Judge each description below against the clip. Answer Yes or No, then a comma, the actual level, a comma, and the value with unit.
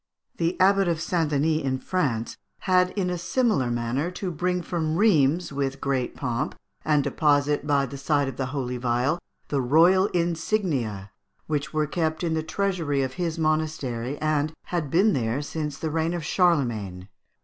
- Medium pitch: Yes, medium, 155 Hz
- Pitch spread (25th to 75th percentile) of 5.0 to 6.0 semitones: No, average, 4.3 semitones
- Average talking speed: Yes, average, 170 wpm